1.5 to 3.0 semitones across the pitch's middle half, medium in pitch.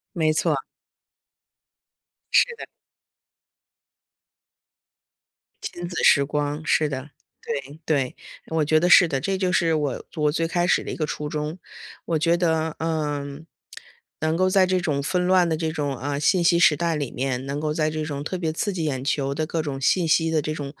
Yes: narrow, 2.6 semitones; medium, 155 Hz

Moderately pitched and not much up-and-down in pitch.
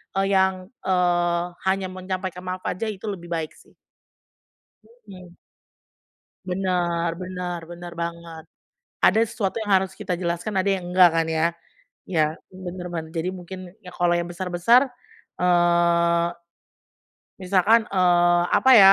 Yes: medium, 180 Hz; narrow, 1.6 semitones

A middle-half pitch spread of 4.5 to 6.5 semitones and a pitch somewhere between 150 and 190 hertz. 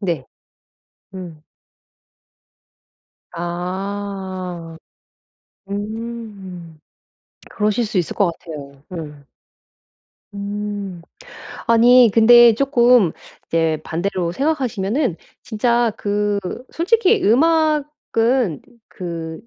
No: wide, 5.4 semitones; high, 205 Hz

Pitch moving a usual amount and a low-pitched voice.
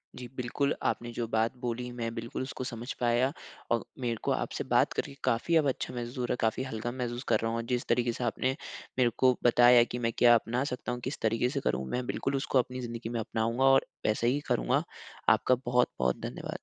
No: narrow, 1.6 semitones; low, 120 Hz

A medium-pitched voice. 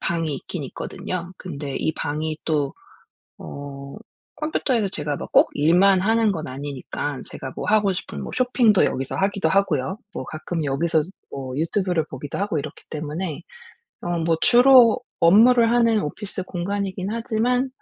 Yes: medium, 175 Hz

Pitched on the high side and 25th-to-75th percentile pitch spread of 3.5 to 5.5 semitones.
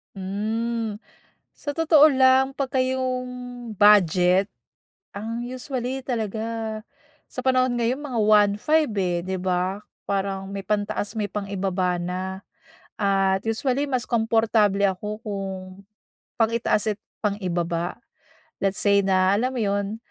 Yes: high, 210 Hz; average, 4.0 semitones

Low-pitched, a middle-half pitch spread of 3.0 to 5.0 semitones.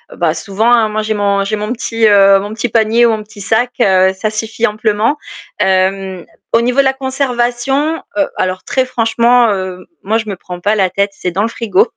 No: high, 215 Hz; average, 3.3 semitones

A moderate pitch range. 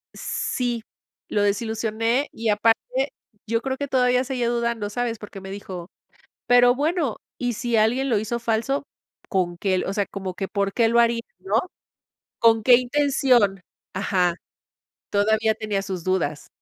Yes: average, 3.6 semitones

